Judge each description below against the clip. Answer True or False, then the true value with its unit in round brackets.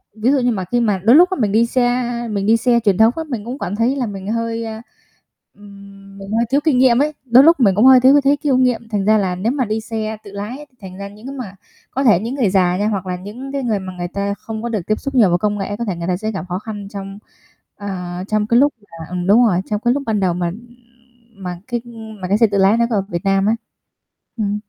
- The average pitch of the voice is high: True (215 Hz)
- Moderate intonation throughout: True (3.7 semitones)